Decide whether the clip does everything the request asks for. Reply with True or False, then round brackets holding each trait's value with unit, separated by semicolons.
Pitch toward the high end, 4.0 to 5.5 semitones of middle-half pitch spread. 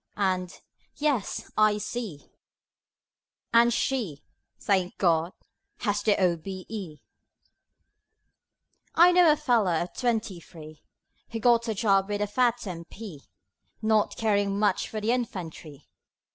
True (205 Hz; 4.4 semitones)